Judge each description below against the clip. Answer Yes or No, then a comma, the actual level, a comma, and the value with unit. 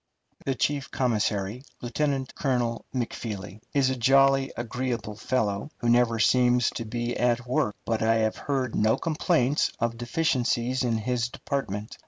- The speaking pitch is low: Yes, low, 120 Hz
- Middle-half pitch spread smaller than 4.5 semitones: Yes, narrow, 2.6 semitones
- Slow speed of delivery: No, average, 145 wpm